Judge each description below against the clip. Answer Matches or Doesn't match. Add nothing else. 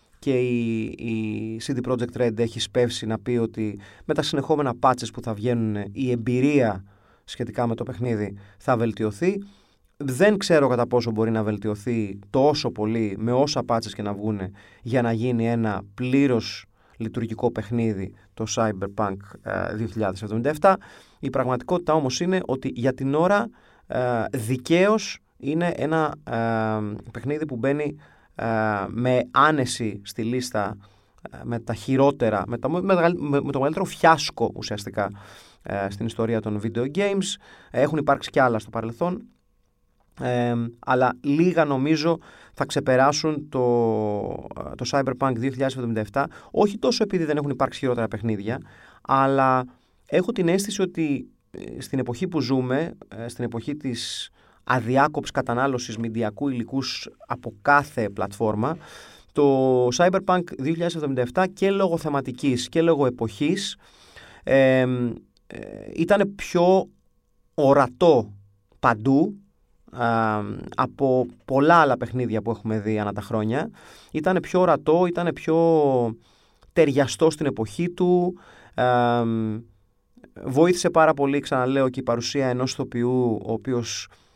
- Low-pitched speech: Matches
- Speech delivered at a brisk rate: Doesn't match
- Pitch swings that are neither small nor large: Matches